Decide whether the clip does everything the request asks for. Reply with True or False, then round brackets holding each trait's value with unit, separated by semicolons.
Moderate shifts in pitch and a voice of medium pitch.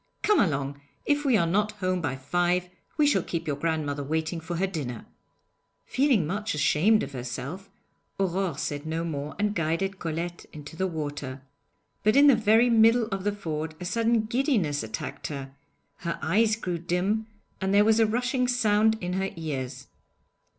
False (5.7 semitones; 180 Hz)